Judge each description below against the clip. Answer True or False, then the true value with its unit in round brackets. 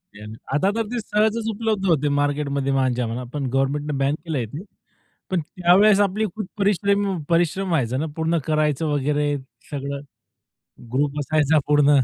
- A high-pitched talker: False (150 Hz)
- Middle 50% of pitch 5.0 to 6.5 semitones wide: True (5.5 semitones)